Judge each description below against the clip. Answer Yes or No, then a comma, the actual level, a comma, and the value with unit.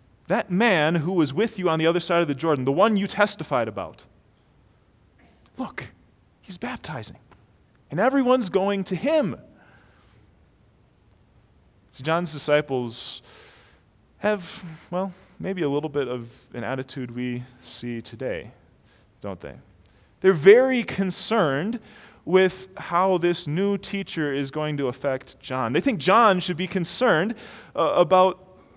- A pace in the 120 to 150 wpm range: Yes, slow, 135 wpm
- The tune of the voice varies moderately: No, wide, 7.0 semitones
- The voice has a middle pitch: Yes, medium, 165 Hz